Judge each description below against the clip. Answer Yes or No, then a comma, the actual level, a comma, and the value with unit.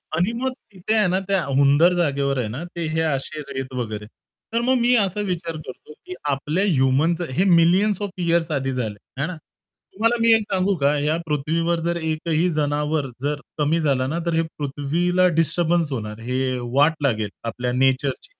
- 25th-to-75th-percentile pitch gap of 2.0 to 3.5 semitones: No, average, 4.3 semitones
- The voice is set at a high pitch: No, medium, 155 Hz